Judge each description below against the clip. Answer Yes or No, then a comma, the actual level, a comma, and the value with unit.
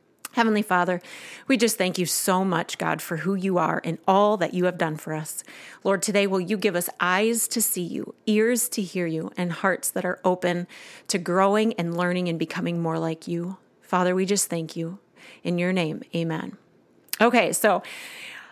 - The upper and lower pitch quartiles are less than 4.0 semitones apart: Yes, average, 2.9 semitones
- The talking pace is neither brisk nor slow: Yes, average, 195 wpm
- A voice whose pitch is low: No, medium, 180 Hz